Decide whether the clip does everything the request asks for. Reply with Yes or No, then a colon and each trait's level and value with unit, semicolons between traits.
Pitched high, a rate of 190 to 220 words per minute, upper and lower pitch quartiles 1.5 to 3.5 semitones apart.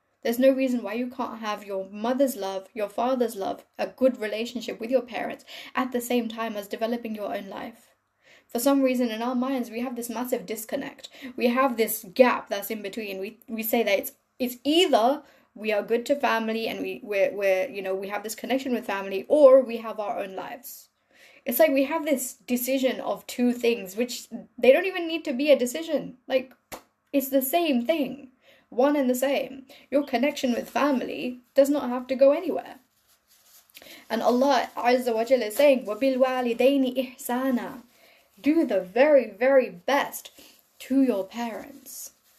No: very high, 250 Hz; average, 180 wpm; average, 3.1 semitones